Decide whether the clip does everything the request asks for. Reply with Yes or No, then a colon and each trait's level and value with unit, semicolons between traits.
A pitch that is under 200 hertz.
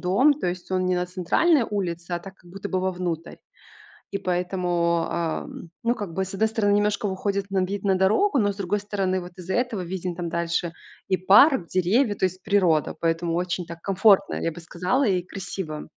Yes: medium, 185 Hz